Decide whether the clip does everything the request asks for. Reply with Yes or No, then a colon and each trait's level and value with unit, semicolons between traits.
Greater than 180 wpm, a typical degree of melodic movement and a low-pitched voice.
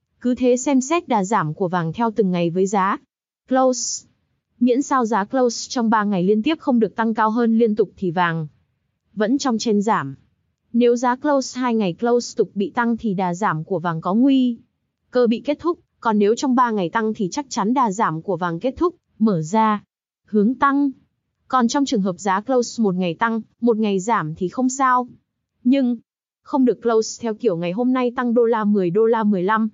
No: average, 215 wpm; average, 4.3 semitones; high, 225 Hz